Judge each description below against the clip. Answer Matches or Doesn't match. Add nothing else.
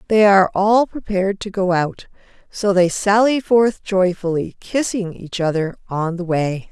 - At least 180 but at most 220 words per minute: Doesn't match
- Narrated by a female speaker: Matches